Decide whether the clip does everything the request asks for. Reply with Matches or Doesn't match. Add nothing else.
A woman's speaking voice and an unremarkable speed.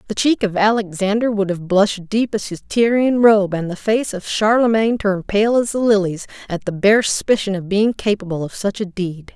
Doesn't match